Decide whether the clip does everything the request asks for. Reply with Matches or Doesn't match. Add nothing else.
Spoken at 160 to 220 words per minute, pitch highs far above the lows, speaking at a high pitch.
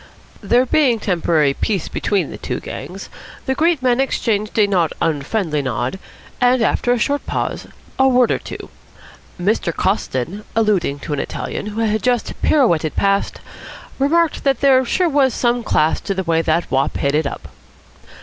Matches